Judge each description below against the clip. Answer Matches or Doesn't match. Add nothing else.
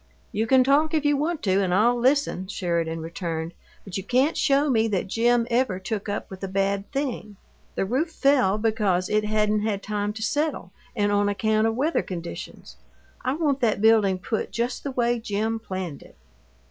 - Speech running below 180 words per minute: Doesn't match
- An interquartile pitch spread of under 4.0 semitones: Doesn't match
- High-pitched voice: Matches